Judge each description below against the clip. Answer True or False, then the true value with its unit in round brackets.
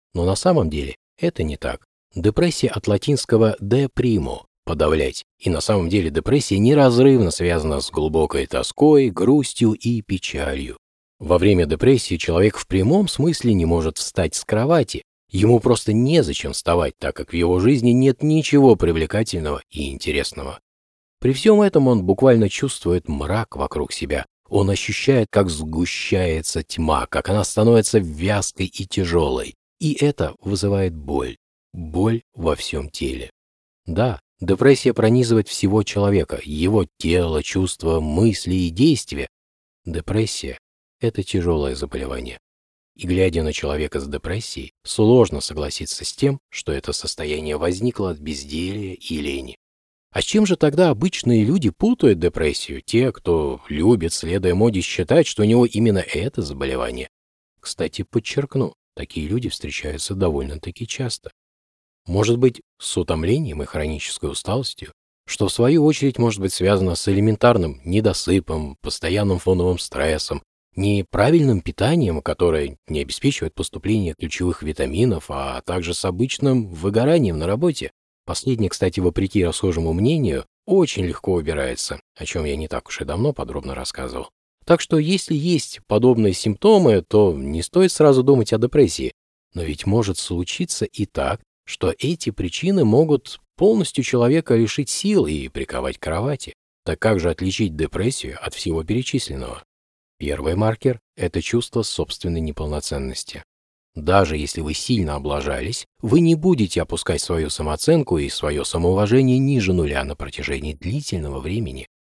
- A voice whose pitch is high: False (95 Hz)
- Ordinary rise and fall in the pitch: False (7.5 semitones)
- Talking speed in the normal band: True (140 wpm)